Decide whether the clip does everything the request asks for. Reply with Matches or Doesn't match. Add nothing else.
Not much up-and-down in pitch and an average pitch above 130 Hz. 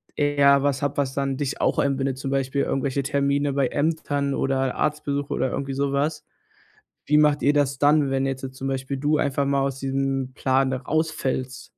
Matches